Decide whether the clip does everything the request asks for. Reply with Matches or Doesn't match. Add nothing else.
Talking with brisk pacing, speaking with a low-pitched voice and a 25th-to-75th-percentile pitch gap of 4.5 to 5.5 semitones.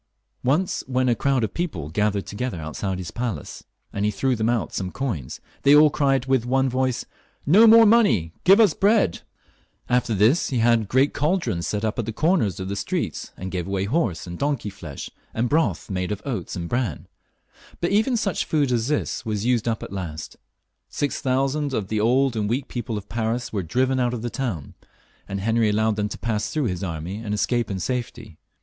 Matches